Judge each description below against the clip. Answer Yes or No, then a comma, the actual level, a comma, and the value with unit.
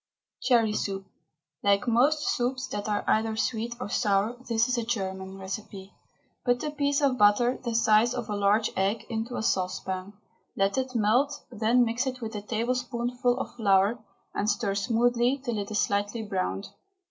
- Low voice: No, high, 225 Hz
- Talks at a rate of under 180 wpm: Yes, average, 170 wpm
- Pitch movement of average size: Yes, average, 3.2 semitones